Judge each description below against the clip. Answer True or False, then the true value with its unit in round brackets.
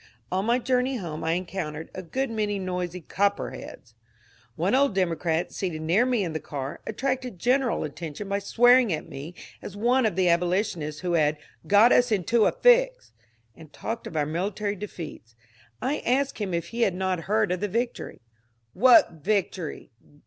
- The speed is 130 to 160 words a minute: False (180 wpm)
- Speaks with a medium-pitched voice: False (195 Hz)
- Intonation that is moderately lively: False (5.8 semitones)